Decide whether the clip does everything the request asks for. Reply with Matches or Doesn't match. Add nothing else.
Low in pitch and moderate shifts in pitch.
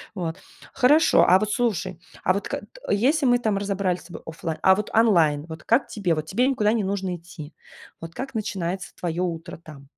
Doesn't match